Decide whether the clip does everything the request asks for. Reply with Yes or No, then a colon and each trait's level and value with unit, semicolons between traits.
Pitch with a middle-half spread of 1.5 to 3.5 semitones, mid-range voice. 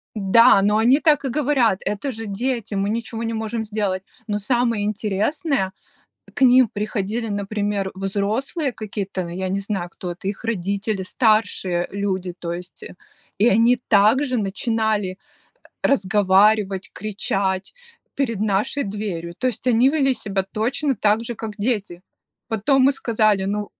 No: average, 3.1 semitones; high, 210 Hz